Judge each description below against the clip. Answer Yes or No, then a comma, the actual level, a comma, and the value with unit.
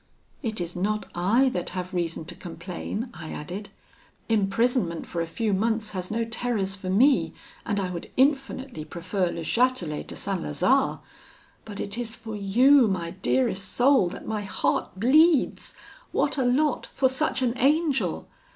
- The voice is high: Yes, high, 210 Hz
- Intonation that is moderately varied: No, wide, 5.8 semitones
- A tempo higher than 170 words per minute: No, average, 160 wpm